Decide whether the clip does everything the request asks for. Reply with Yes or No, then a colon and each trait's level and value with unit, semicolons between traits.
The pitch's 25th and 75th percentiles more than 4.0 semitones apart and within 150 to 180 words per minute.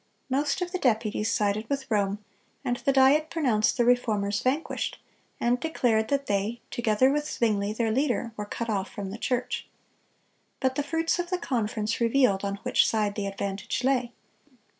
Yes: average, 4.5 semitones; average, 170 wpm